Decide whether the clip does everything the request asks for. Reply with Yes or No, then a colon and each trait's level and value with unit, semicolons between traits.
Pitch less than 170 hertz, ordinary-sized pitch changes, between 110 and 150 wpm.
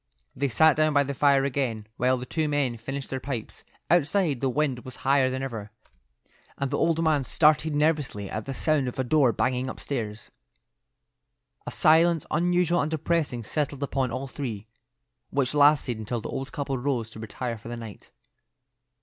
No: low, 135 Hz; average, 3.5 semitones; average, 175 wpm